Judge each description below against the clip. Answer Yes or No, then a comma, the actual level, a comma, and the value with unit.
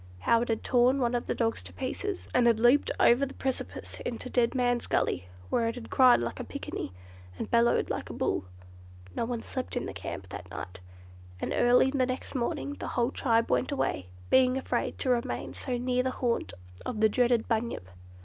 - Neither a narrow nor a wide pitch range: No, narrow, 1.8 semitones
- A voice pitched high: Yes, high, 245 Hz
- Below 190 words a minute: No, fast, 205 wpm